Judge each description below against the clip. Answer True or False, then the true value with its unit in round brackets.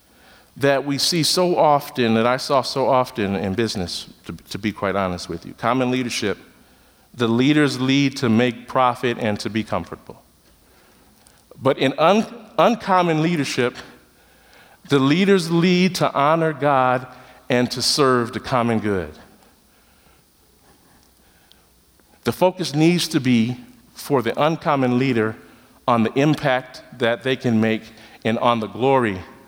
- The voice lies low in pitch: True (125 Hz)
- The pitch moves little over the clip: False (4.3 semitones)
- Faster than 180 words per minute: False (140 wpm)